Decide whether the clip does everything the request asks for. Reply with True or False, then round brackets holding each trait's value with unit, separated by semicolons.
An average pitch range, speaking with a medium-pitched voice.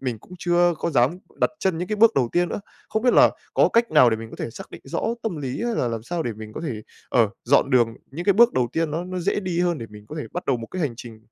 False (7.0 semitones; 155 Hz)